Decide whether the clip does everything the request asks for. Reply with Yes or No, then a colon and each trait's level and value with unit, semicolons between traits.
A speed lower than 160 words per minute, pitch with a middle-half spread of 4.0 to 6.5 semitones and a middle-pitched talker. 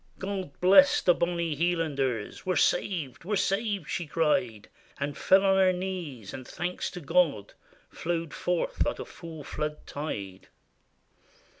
Yes: average, 150 wpm; average, 4.4 semitones; medium, 165 Hz